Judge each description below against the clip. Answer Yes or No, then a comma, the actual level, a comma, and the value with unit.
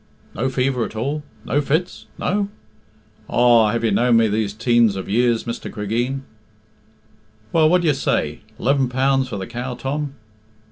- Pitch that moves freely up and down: No, average, 3.7 semitones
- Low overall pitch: Yes, low, 120 Hz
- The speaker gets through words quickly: No, average, 160 wpm